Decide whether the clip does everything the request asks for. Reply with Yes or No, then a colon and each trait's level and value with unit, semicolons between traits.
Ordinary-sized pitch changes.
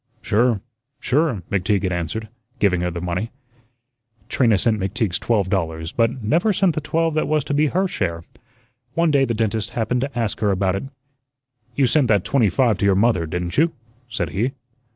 No: wide, 6.2 semitones